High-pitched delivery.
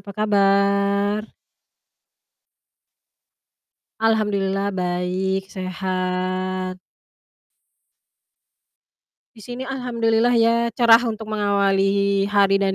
Yes: high, 200 Hz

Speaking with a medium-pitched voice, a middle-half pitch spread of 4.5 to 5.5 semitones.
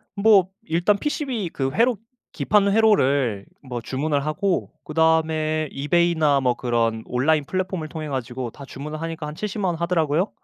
Yes: medium, 155 Hz; average, 5.2 semitones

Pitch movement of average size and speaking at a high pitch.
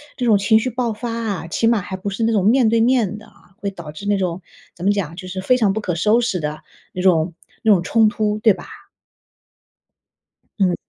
Yes: average, 3.6 semitones; high, 205 Hz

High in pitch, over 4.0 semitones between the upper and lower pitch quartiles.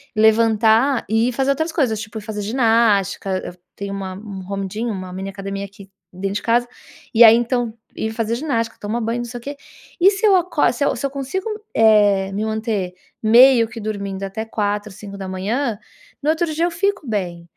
No: high, 220 Hz; average, 3.5 semitones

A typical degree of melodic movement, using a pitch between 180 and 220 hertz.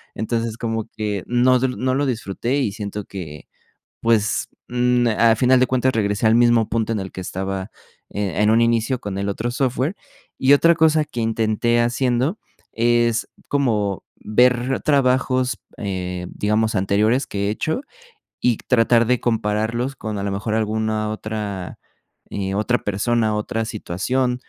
No: average, 3.0 semitones; low, 115 Hz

